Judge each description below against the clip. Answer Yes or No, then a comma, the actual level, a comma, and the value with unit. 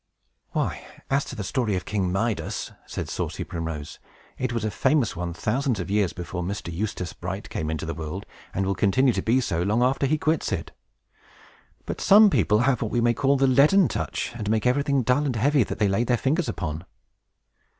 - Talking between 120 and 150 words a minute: No, fast, 205 wpm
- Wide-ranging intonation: Yes, wide, 6.1 semitones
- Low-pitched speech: Yes, low, 110 Hz